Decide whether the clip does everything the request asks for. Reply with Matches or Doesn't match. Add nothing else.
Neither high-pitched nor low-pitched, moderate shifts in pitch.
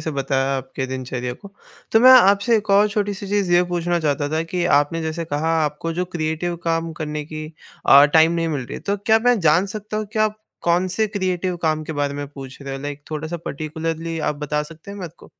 Matches